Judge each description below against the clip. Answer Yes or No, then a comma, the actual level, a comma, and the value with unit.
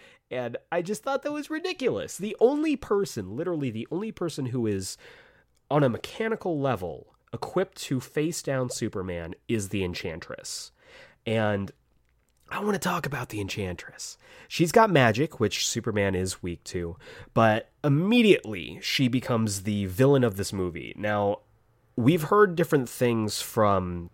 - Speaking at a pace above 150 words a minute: No, average, 145 wpm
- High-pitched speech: No, low, 125 Hz